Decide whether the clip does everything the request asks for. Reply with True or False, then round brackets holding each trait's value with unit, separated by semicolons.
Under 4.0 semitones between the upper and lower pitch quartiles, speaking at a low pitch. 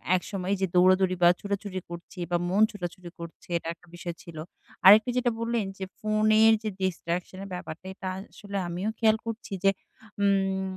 False (3.1 semitones; 190 Hz)